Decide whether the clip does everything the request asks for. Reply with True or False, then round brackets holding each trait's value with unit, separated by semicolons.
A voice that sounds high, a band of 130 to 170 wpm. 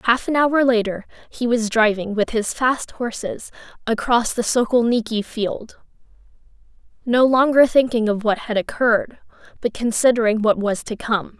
True (230 Hz; 145 wpm)